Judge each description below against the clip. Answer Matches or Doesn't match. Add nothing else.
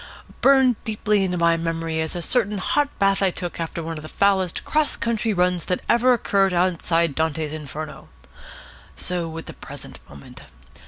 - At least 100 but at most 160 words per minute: Doesn't match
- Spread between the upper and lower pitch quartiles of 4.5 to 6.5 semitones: Doesn't match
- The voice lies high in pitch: Doesn't match